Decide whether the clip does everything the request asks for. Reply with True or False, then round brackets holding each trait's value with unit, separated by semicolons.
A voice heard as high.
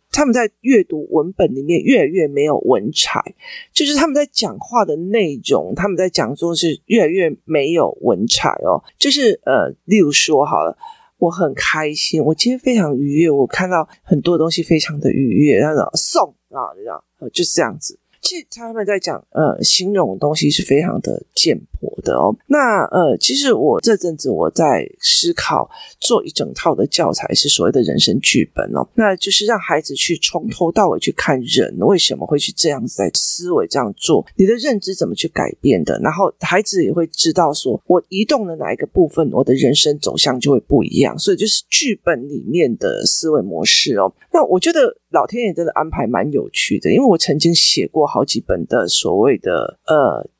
True (195 Hz)